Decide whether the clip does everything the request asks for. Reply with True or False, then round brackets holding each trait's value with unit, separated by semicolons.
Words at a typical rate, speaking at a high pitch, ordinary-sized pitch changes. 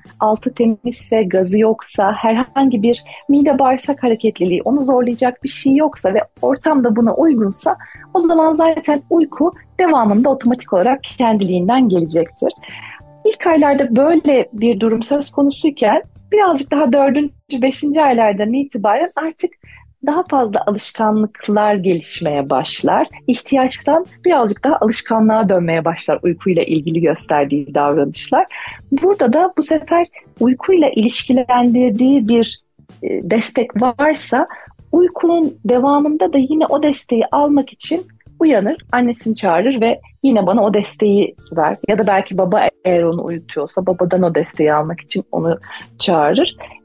False (125 wpm; 245 Hz; 5.7 semitones)